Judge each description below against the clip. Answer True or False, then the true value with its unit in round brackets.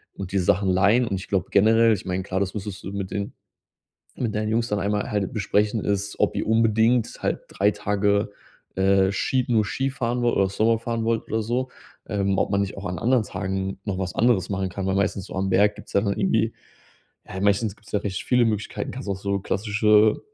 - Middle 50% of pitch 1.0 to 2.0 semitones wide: False (2.4 semitones)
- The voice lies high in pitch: False (105 Hz)